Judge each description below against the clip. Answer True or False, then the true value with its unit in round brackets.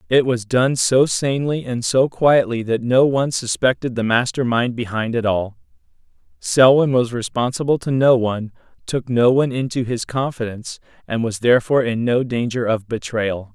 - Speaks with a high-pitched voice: False (120 Hz)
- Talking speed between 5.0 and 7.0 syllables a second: True (5.1 syllables/s)